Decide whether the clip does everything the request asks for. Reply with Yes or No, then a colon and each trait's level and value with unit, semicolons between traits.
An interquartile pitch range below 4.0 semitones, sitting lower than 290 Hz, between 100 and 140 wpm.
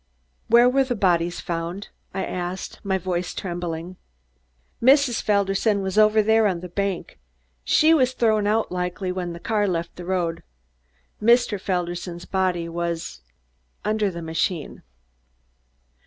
Yes: average, 3.6 semitones; high, 190 Hz; slow, 135 wpm